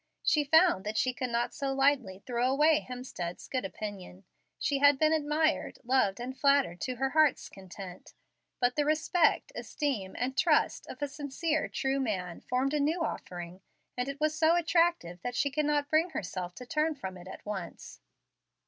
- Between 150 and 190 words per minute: Yes, average, 180 wpm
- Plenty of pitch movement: Yes, wide, 6.4 semitones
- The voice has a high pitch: Yes, very high, 270 Hz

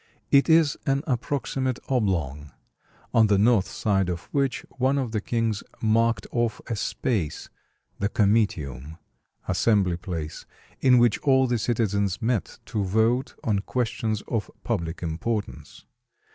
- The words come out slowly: Yes, slow, 130 wpm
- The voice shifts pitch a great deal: No, average, 4.1 semitones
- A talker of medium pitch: No, low, 110 Hz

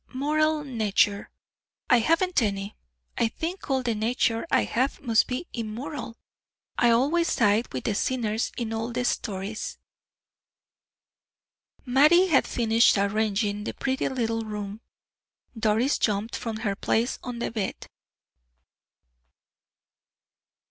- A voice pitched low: No, high, 230 Hz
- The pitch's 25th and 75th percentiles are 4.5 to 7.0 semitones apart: No, average, 3.6 semitones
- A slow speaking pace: Yes, slow, 115 wpm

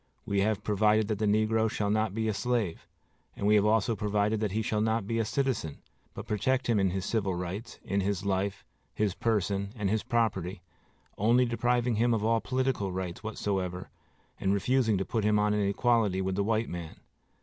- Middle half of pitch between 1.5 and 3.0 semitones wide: Yes, narrow, 2.4 semitones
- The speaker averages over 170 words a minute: Yes, average, 200 wpm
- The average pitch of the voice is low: Yes, low, 105 Hz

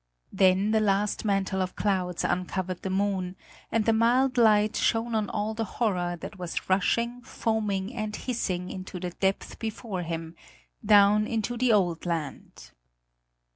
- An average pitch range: Yes, average, 3.1 semitones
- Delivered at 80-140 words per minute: No, average, 150 wpm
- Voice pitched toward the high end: Yes, high, 200 Hz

